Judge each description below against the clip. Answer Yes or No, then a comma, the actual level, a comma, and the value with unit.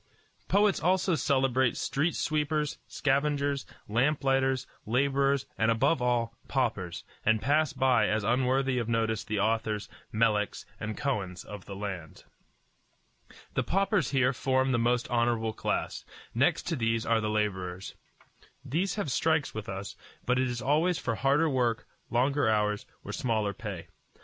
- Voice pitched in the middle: No, low, 125 Hz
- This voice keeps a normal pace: Yes, average, 150 wpm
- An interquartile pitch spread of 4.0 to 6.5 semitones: Yes, average, 4.4 semitones